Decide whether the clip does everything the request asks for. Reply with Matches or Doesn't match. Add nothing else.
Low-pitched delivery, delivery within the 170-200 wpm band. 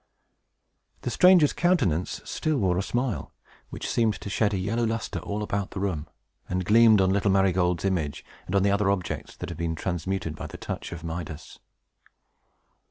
Matches